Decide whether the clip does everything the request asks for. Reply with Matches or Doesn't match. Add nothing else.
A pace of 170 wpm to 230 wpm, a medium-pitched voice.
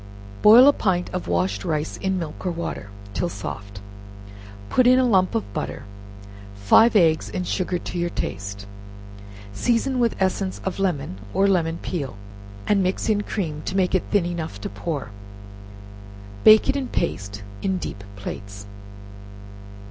Doesn't match